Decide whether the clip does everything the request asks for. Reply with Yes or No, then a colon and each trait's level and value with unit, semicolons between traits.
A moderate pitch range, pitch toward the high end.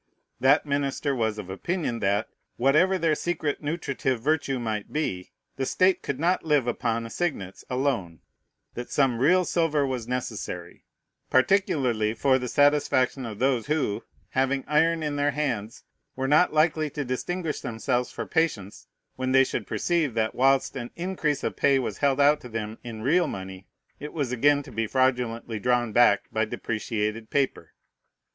No: average, 4.5 semitones; low, 135 Hz